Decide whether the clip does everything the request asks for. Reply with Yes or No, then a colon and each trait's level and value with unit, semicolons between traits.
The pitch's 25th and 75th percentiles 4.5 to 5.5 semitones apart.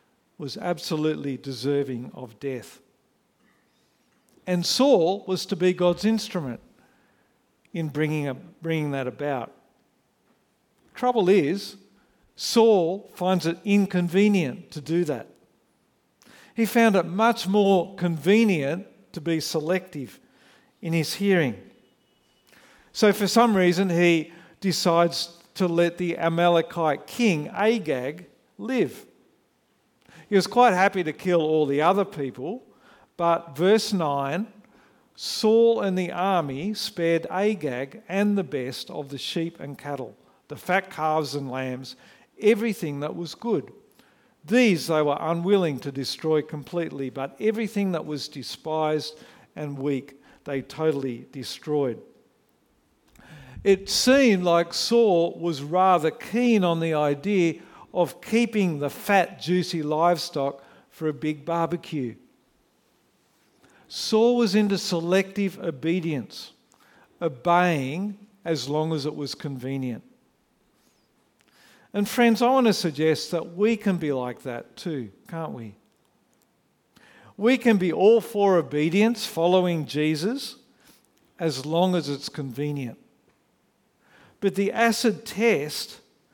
Yes: average, 5.0 semitones